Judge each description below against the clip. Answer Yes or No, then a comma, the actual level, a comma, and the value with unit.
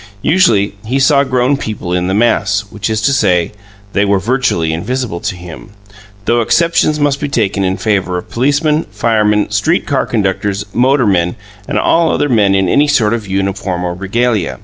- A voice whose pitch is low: Yes, low, 105 Hz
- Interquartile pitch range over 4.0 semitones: Yes, wide, 5.4 semitones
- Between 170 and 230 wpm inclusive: Yes, average, 175 wpm